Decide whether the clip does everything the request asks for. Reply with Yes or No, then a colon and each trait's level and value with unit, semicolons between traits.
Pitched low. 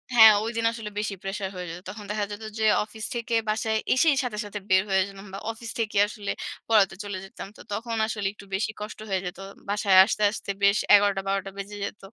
No: high, 210 Hz